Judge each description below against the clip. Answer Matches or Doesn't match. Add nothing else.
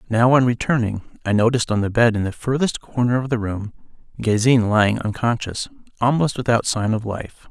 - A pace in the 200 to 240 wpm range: Doesn't match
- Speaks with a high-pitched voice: Doesn't match